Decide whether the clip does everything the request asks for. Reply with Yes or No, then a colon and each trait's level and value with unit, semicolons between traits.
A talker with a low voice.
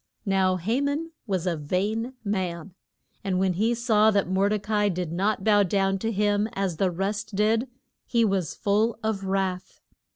No: high, 200 Hz